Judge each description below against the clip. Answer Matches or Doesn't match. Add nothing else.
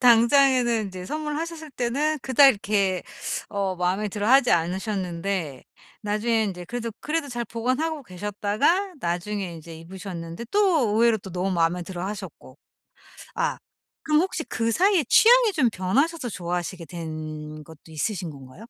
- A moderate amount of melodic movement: Doesn't match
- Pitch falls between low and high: Doesn't match